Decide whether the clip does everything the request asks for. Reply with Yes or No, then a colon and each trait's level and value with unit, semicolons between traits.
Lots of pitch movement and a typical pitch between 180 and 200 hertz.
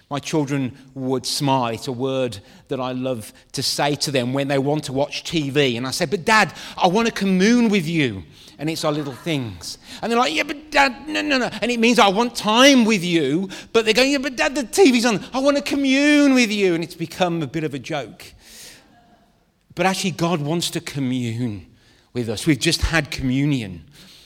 No: wide, 8.9 semitones; medium, 160 Hz